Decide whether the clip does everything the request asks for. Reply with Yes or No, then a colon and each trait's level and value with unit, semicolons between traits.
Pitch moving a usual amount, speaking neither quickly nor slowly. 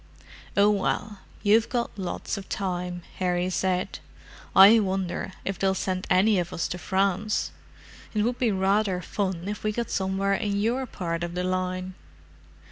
No: narrow, 2.3 semitones; average, 155 wpm